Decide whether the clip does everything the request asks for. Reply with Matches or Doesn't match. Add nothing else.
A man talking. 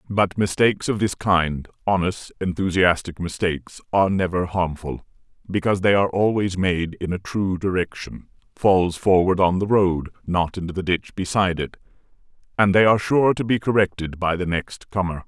Matches